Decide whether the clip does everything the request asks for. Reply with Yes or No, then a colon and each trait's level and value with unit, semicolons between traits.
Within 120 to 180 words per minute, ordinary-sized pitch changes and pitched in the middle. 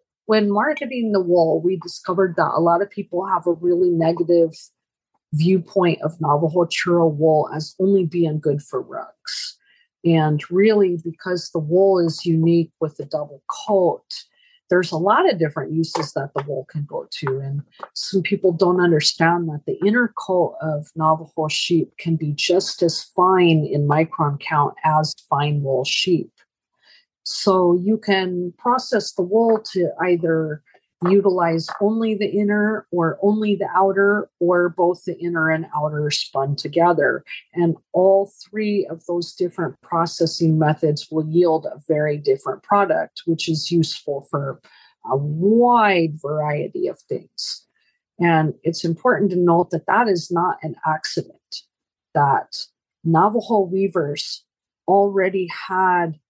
Yes: average, 145 wpm; average, 3.5 semitones; medium, 175 Hz